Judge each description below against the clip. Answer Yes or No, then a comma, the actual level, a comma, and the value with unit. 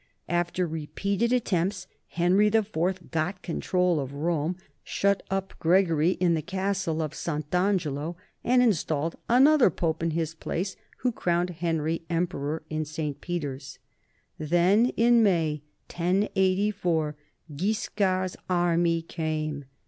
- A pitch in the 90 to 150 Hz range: No, medium, 175 Hz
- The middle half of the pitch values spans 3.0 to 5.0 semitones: Yes, average, 3.4 semitones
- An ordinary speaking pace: No, slow, 120 wpm